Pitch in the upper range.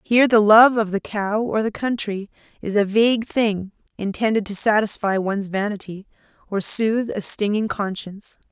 Yes: high, 210 Hz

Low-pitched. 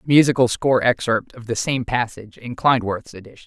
Yes: low, 120 Hz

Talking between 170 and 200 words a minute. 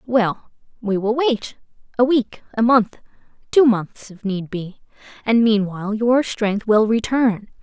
No: slow, 135 wpm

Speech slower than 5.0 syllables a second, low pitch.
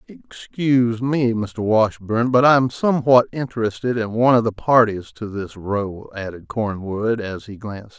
Yes: 4.8 syllables/s; low, 110 Hz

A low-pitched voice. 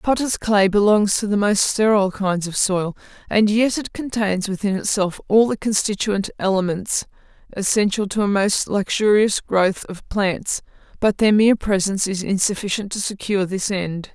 No: high, 200 Hz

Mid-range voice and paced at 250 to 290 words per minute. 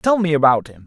Yes: medium, 155 Hz; fast, 275 wpm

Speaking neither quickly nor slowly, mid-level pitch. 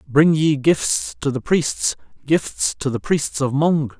Yes: average, 180 wpm; medium, 145 Hz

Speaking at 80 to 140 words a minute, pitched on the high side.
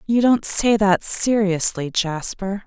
Yes: slow, 135 wpm; high, 200 Hz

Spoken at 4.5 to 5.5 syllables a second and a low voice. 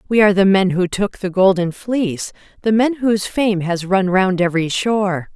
No: 5.2 syllables/s; high, 195 Hz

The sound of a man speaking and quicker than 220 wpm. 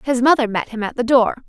No: female; fast, 285 wpm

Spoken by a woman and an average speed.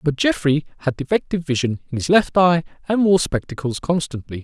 No: male; average, 175 wpm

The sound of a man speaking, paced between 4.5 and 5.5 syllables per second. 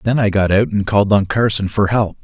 No: male; 5.8 syllables/s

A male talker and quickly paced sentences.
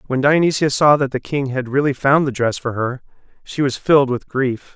Yes: male; fast, 225 wpm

